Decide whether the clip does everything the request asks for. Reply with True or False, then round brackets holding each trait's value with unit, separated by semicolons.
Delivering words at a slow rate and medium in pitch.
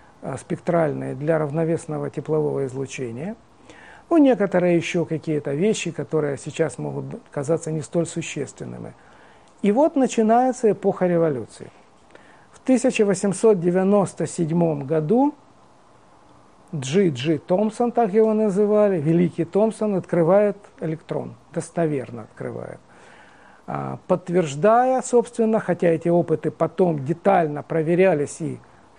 True (95 wpm; 170 Hz)